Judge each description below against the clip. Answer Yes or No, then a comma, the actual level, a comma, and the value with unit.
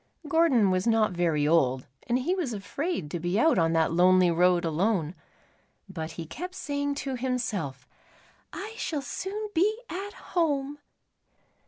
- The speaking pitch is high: Yes, high, 220 Hz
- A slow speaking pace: No, average, 150 wpm